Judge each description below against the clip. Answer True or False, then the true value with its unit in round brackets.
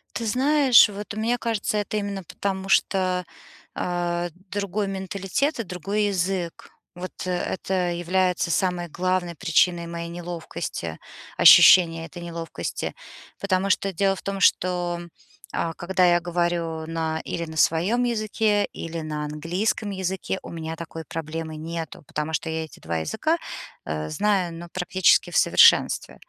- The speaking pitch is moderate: True (180 Hz)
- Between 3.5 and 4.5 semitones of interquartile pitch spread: False (2.9 semitones)